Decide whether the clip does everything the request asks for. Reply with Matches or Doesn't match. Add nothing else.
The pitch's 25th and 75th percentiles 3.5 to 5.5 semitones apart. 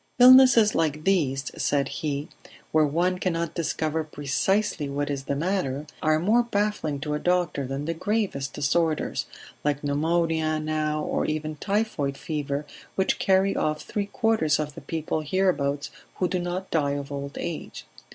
Matches